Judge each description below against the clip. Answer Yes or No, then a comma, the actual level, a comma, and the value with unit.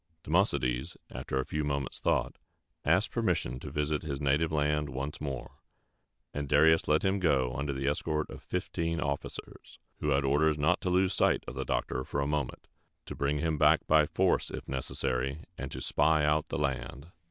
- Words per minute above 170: Yes, average, 185 wpm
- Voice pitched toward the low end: Yes, very low, 75 Hz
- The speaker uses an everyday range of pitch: No, narrow, 2.3 semitones